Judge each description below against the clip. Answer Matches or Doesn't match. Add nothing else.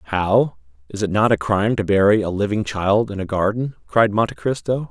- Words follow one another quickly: Matches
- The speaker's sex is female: Doesn't match